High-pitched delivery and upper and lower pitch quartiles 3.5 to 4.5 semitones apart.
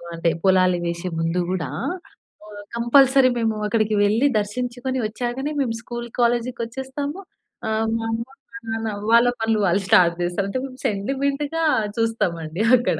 Yes: high, 225 Hz; average, 4.1 semitones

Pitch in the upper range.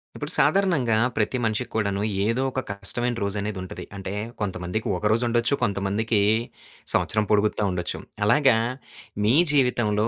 No: low, 110 Hz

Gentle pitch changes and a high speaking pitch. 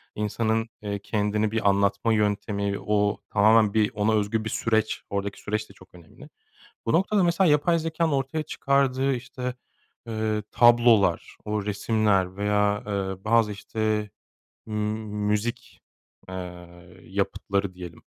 No: narrow, 2.2 semitones; low, 105 Hz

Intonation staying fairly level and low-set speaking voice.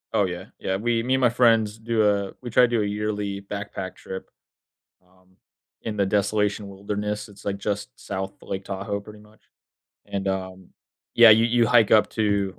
Yes: narrow, 2.0 semitones; low, 105 Hz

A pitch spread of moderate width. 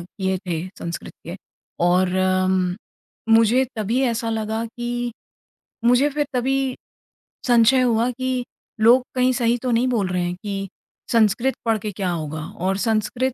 Yes: average, 4.2 semitones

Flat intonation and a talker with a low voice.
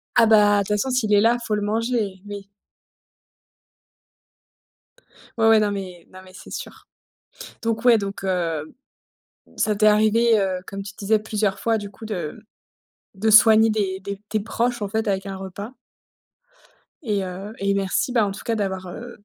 No: narrow, 2.2 semitones; high, 205 Hz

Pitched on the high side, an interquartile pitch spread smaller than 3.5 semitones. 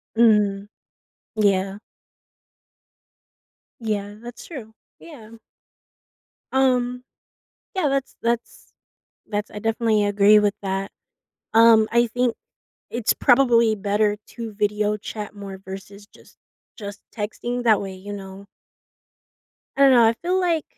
Yes: high, 215 Hz; average, 2.8 semitones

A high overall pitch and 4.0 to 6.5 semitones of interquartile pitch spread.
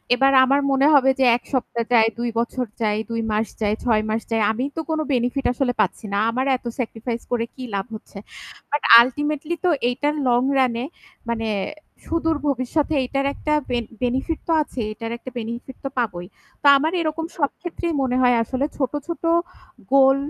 No: very high, 255 Hz; average, 3.5 semitones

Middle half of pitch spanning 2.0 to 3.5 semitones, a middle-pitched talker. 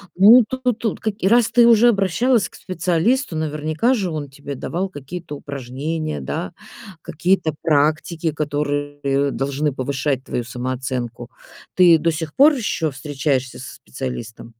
No: average, 5.2 semitones; medium, 155 Hz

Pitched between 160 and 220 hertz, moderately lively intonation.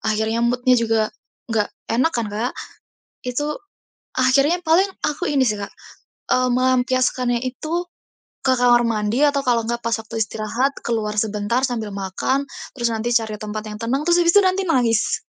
No: high, 245 Hz; average, 3.5 semitones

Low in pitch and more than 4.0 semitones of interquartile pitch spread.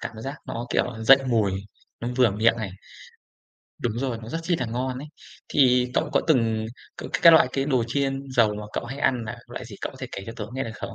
No: low, 120 Hz; average, 3.2 semitones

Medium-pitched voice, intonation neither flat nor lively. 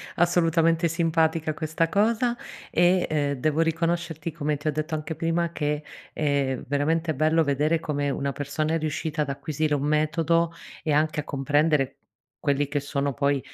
No: medium, 155 Hz; narrow, 2.3 semitones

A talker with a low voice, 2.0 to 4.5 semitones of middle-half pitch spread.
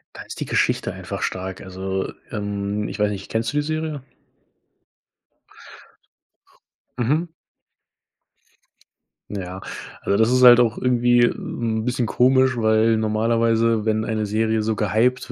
Yes: low, 110 Hz; average, 2.7 semitones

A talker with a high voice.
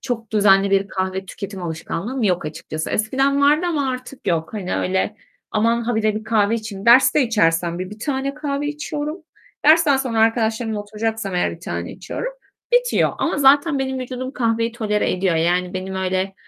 Yes: high, 220 Hz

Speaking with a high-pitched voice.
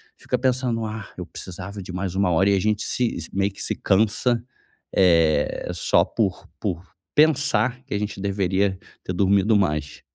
No: low, 100 Hz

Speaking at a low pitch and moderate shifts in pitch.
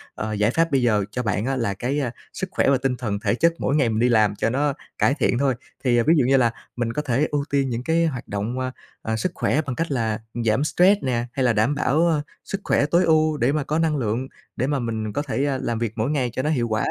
Yes: low, 130 Hz; average, 4.2 semitones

